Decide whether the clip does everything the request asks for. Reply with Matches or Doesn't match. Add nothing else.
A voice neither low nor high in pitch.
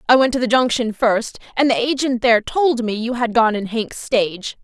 Doesn't match